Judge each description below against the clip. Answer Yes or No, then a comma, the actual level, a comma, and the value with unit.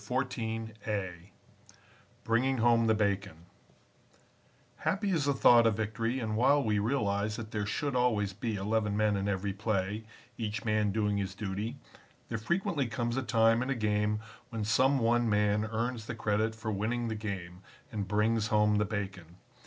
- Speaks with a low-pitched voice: Yes, low, 110 Hz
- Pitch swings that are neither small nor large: No, narrow, 2.2 semitones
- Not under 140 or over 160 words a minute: No, average, 170 wpm